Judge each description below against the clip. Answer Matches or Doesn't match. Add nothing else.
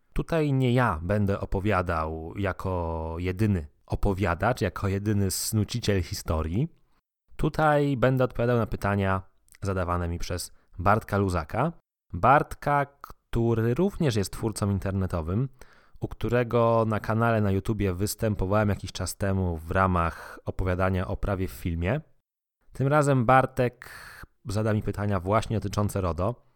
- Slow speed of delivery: Doesn't match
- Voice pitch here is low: Matches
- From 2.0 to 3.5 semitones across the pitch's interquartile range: Doesn't match